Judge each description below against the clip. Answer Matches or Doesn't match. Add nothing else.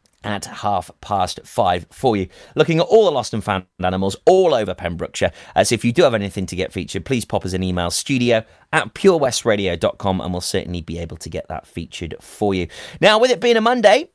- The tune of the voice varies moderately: Doesn't match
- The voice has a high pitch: Doesn't match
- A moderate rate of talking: Doesn't match